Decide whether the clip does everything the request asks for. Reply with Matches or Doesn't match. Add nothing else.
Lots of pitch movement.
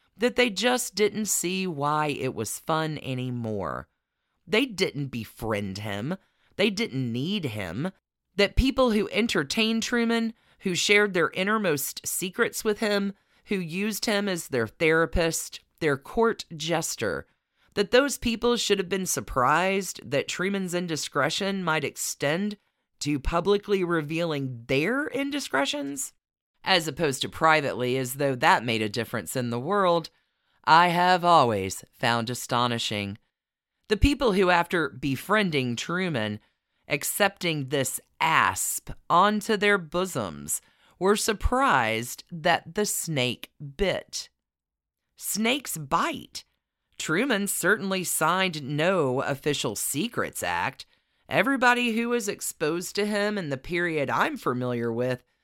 Matches